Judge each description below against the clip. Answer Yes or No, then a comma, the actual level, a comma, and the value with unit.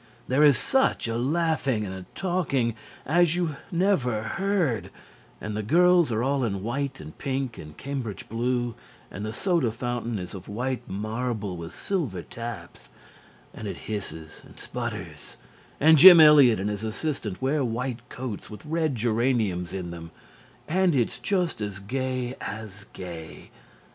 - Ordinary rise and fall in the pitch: No, wide, 5.7 semitones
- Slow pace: No, average, 155 wpm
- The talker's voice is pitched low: Yes, low, 120 Hz